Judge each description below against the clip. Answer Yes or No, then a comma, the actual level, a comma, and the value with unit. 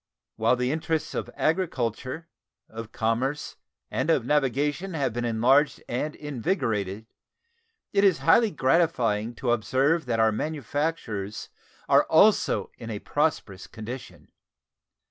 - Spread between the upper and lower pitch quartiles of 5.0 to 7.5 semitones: Yes, wide, 5.5 semitones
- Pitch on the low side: Yes, low, 130 Hz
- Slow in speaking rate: Yes, slow, 120 wpm